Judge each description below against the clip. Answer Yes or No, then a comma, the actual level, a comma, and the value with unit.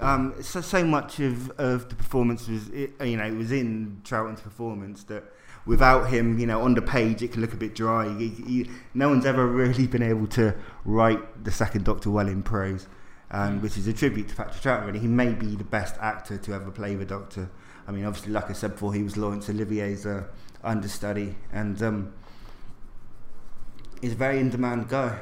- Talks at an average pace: No, fast, 210 wpm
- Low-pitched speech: Yes, low, 110 Hz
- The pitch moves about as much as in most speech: Yes, average, 3.1 semitones